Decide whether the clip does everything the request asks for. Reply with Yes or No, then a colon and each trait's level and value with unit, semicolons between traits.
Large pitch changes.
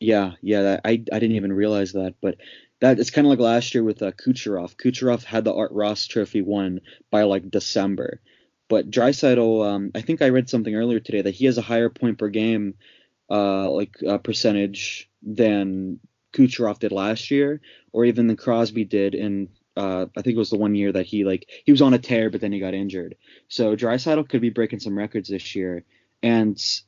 No: average, 2.8 semitones